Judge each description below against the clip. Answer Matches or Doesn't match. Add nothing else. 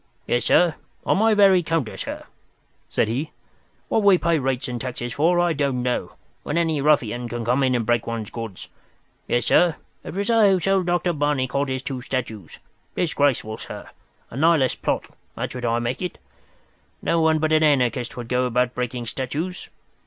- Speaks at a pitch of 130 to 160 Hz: Matches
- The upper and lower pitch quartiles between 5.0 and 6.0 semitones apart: Matches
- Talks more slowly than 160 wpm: Doesn't match